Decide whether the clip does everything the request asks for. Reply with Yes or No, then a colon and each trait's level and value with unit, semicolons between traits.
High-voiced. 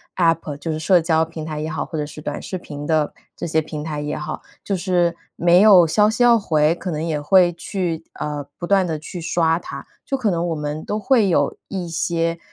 No: medium, 165 Hz